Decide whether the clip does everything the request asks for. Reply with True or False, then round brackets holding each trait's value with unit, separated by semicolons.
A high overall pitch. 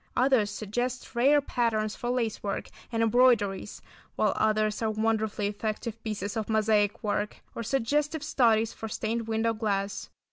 True (220 Hz)